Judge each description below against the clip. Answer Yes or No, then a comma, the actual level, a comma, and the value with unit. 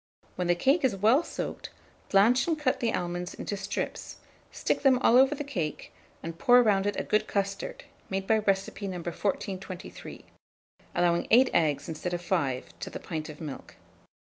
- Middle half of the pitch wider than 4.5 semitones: Yes, average, 5.3 semitones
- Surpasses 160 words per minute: Yes, average, 175 wpm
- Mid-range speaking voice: No, high, 195 Hz